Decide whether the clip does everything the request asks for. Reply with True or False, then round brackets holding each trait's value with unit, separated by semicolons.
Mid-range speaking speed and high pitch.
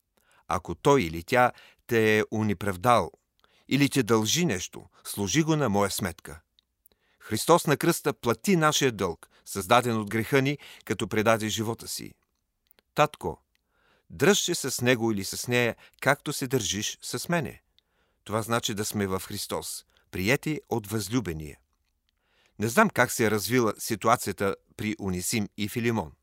False (145 wpm; 115 Hz)